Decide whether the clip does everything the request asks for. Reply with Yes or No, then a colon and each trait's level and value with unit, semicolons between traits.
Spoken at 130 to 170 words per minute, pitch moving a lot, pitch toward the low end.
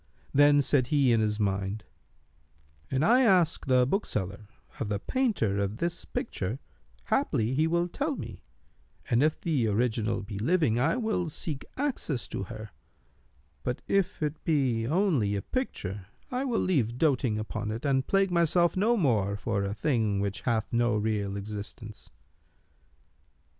Yes: average, 155 wpm; wide, 7.7 semitones; low, 125 Hz